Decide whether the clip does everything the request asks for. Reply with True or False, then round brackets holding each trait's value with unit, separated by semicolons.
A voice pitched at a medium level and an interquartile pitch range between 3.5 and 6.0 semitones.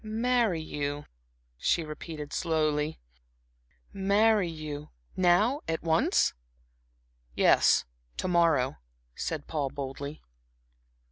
True (160 Hz; 4.1 semitones)